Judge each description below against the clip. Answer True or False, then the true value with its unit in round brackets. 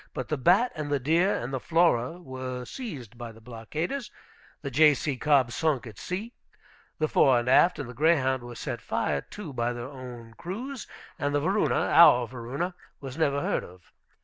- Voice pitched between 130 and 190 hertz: True (135 Hz)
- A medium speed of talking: True (185 wpm)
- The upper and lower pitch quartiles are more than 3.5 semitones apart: True (5.2 semitones)